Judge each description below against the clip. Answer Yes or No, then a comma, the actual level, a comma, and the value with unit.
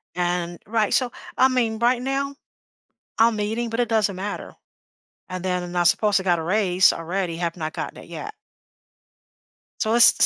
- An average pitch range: Yes, average, 4.6 semitones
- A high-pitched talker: Yes, high, 205 Hz